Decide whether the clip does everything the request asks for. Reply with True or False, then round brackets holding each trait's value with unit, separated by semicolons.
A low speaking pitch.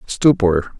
True (110 Hz)